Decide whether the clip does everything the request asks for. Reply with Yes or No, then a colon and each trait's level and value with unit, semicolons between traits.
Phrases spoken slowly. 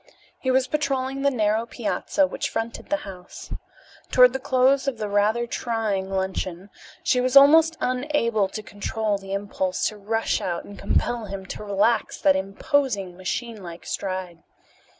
No: average, 155 wpm